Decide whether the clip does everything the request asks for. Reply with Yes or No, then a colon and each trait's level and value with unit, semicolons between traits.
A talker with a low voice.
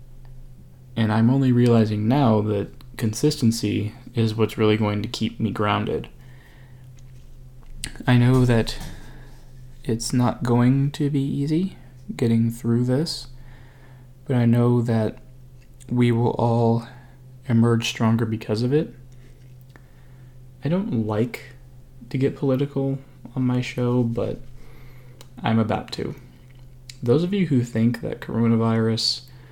Yes: low, 125 Hz